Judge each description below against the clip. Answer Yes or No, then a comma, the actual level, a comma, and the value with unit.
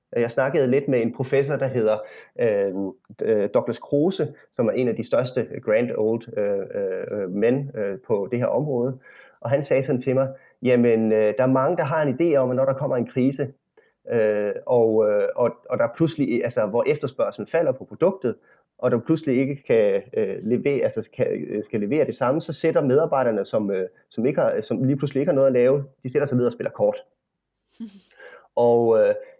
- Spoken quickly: No, average, 205 wpm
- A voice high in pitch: No, medium, 140 Hz